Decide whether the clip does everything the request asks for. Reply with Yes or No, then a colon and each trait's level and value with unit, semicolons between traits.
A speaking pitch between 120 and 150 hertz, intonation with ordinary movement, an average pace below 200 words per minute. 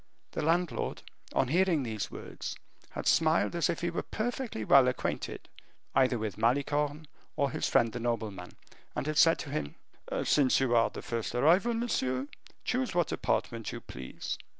No: medium, 140 Hz; wide, 6.3 semitones; average, 165 wpm